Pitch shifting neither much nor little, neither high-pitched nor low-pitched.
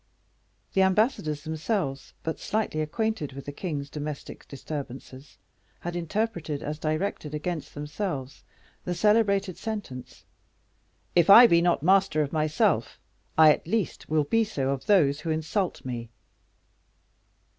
Yes: average, 5.0 semitones; medium, 160 Hz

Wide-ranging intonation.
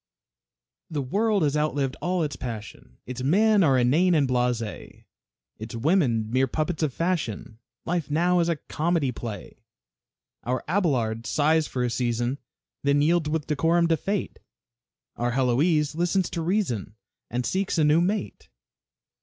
Yes: wide, 5.7 semitones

